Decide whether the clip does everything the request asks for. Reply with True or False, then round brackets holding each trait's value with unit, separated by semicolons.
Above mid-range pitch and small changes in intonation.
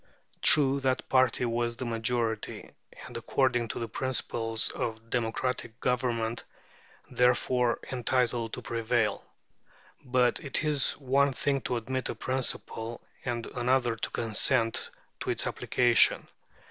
False (120 Hz; 2.0 semitones)